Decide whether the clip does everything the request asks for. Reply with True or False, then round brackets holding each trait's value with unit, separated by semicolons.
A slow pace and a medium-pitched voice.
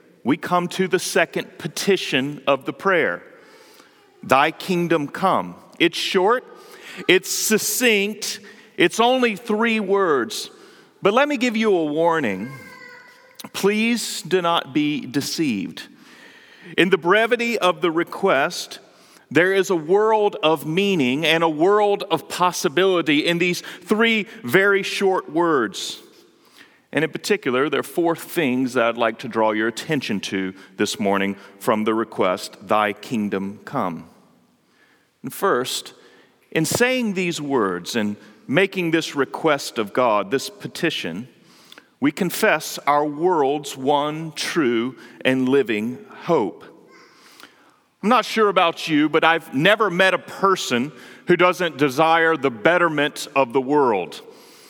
True (130 wpm; 180 Hz)